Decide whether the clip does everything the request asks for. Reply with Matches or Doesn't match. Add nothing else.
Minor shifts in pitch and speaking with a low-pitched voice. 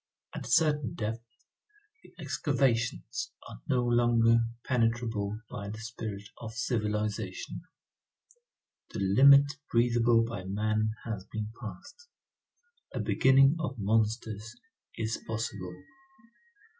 Matches